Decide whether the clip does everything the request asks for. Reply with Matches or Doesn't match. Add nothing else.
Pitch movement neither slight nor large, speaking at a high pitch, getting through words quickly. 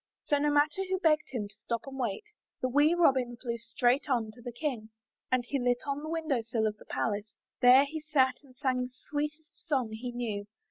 Matches